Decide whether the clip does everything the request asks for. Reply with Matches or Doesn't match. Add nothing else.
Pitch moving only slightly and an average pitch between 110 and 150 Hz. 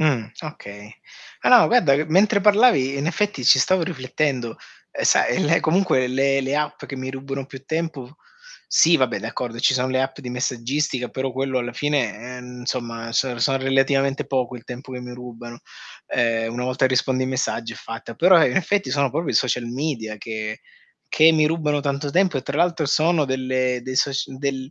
Doesn't match